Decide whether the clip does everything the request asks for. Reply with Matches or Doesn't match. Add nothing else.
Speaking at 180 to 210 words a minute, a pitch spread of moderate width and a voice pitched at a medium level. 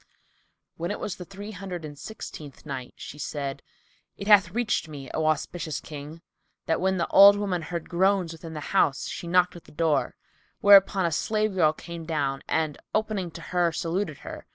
Matches